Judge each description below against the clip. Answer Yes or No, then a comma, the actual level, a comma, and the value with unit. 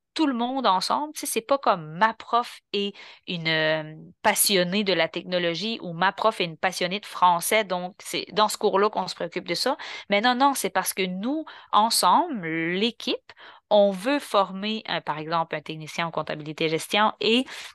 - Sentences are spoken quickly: No, average, 185 wpm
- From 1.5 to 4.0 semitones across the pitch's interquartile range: No, average, 4.4 semitones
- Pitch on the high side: Yes, high, 200 Hz